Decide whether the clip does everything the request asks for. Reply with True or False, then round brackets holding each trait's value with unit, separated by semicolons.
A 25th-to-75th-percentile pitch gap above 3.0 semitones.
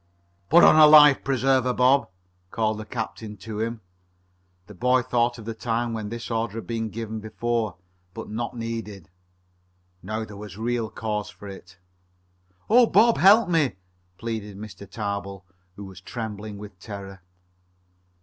False (2.6 semitones)